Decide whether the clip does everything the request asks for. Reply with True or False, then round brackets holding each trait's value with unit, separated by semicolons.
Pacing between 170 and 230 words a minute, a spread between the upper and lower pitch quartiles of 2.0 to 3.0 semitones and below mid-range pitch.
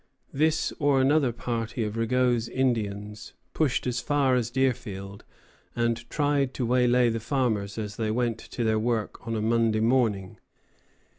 False (155 wpm; 2.7 semitones; 120 Hz)